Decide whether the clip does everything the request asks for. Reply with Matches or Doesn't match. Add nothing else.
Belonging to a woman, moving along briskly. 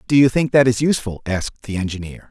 Doesn't match